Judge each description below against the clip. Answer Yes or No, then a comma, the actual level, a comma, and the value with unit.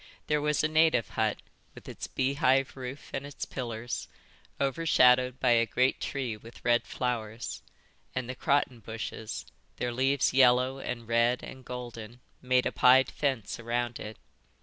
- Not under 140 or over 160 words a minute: Yes, average, 150 wpm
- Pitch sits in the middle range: No, low, 125 Hz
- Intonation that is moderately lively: No, narrow, 2.2 semitones